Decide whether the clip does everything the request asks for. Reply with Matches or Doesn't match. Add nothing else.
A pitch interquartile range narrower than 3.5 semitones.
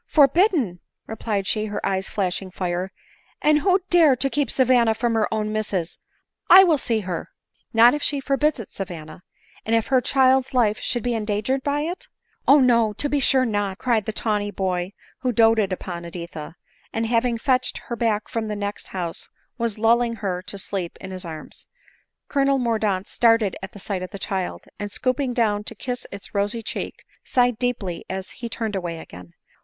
Doesn't match